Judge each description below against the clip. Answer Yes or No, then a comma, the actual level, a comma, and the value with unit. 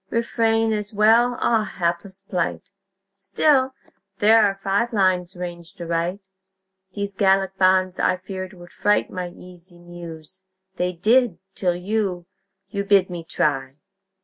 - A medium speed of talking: No, slow, 130 wpm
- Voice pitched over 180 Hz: Yes, high, 190 Hz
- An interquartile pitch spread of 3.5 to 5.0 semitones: No, average, 2.8 semitones